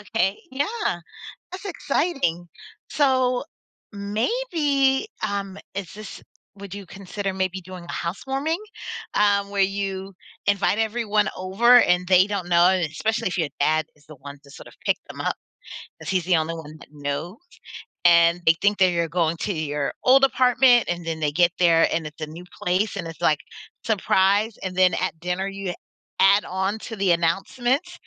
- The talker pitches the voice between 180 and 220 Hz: Yes, high, 190 Hz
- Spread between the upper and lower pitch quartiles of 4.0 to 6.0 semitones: Yes, average, 4.3 semitones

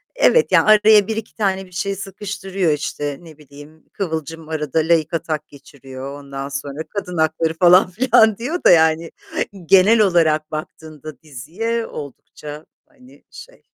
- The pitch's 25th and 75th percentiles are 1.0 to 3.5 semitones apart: No, average, 4.6 semitones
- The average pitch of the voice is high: No, medium, 165 Hz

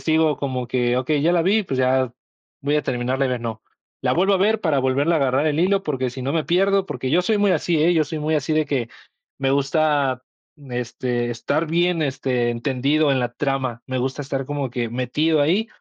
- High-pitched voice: No, medium, 140 Hz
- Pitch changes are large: No, average, 3.8 semitones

